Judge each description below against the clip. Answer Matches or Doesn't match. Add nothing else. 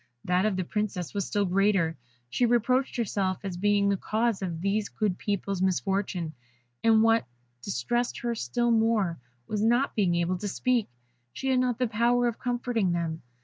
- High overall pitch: Matches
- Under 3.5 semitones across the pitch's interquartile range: Doesn't match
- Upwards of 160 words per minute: Matches